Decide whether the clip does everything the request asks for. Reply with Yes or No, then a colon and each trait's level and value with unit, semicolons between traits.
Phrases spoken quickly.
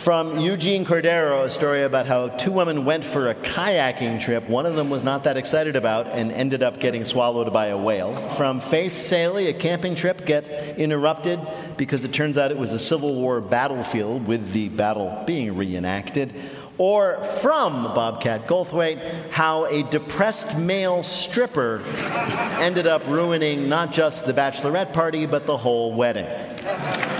No: average, 165 wpm